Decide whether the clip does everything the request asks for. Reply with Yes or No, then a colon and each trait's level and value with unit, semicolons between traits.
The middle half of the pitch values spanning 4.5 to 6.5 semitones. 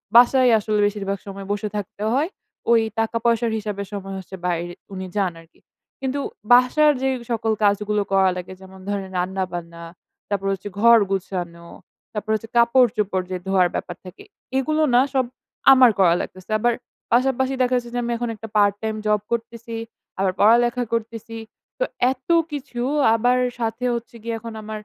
No: average, 3.6 semitones